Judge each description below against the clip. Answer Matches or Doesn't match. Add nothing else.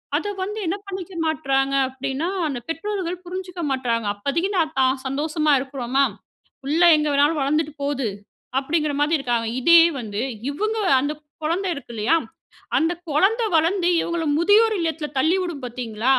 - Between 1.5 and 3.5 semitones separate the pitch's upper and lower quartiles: Doesn't match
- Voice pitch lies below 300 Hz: Doesn't match